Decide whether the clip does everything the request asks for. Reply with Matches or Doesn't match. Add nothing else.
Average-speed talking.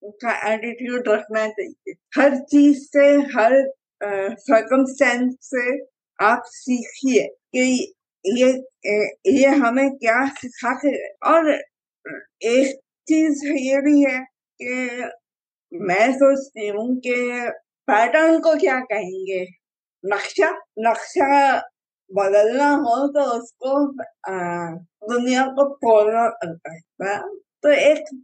Doesn't match